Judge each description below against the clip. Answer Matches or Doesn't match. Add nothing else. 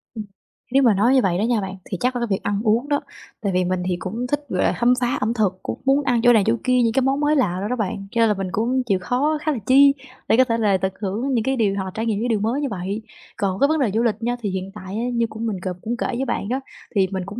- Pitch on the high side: Matches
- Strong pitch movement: Doesn't match